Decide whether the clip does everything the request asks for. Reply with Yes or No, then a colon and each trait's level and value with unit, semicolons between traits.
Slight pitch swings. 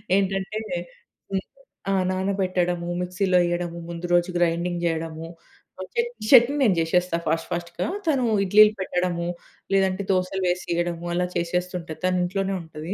Yes: narrow, 1.8 semitones